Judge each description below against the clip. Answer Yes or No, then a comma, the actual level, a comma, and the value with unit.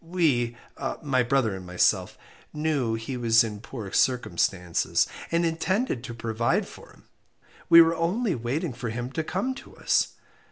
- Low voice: Yes, low, 125 Hz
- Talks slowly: No, average, 155 wpm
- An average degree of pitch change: No, wide, 6.2 semitones